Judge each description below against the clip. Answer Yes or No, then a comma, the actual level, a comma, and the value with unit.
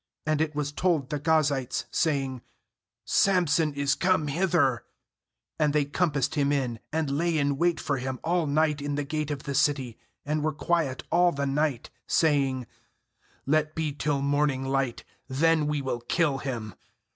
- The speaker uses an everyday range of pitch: No, narrow, 2.3 semitones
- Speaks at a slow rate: No, average, 170 wpm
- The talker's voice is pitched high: No, medium, 145 Hz